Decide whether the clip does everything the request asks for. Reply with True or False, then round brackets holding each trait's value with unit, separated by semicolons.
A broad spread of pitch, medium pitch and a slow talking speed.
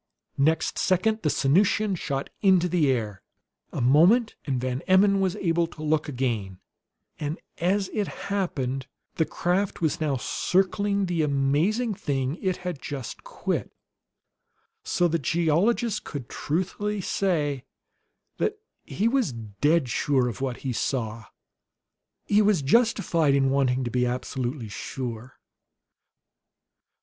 True (6.3 semitones; 155 Hz; 130 wpm)